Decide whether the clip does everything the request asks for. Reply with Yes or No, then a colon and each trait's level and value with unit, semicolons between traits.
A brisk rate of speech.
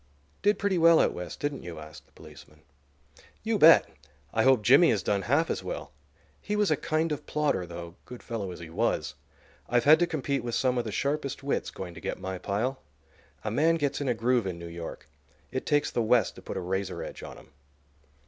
Yes: fast, 220 wpm